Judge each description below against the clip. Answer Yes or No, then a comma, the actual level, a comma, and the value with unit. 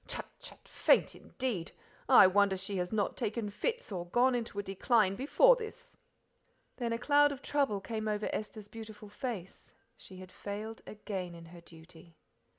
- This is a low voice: No, high, 210 Hz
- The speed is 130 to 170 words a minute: Yes, average, 165 wpm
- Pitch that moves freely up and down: No, average, 4.1 semitones